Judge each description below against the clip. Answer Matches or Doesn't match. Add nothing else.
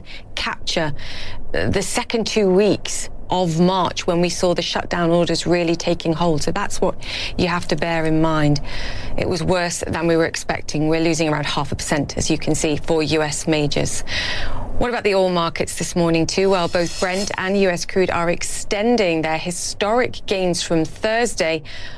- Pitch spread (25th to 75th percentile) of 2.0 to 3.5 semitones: Matches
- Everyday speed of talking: Matches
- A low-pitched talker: Doesn't match